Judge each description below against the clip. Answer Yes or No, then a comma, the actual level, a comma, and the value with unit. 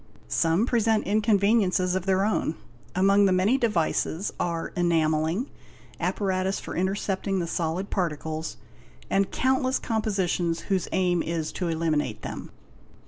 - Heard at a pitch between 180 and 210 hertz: Yes, medium, 185 Hz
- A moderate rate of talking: No, slow, 125 wpm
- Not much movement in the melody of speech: No, average, 3.4 semitones